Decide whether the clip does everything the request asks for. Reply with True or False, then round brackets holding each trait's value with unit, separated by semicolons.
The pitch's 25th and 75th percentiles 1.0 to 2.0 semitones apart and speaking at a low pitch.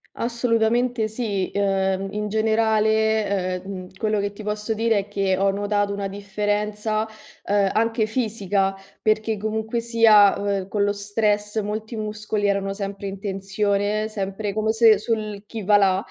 False (1.7 semitones; 210 Hz)